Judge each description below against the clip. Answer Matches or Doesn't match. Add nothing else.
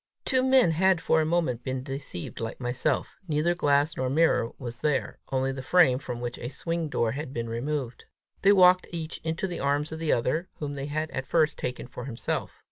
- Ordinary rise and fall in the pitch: Matches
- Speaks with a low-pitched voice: Doesn't match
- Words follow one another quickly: Matches